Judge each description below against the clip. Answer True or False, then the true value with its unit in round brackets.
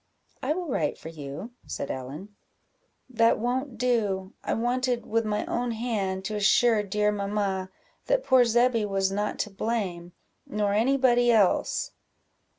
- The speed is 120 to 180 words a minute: True (150 wpm)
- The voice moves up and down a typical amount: True (3.8 semitones)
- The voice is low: False (215 Hz)